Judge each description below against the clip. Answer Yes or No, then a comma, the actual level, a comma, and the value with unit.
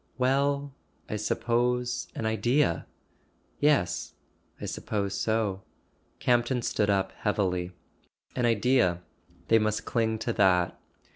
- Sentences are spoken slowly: Yes, slow, 100 wpm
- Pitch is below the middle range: Yes, low, 115 Hz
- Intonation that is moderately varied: Yes, average, 3.5 semitones